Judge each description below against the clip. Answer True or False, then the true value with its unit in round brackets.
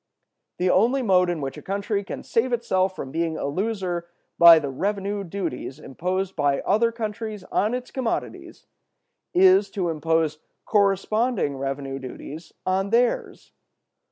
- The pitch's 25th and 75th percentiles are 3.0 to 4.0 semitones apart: False (4.5 semitones)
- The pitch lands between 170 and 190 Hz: True (185 Hz)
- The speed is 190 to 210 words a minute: False (140 wpm)